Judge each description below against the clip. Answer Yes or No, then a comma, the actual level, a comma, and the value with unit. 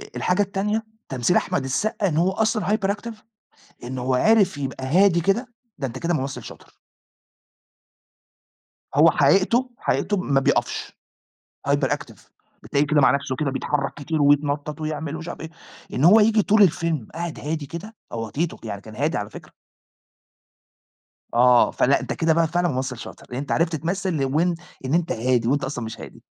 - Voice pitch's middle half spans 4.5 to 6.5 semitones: Yes, wide, 5.5 semitones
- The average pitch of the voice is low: No, medium, 155 Hz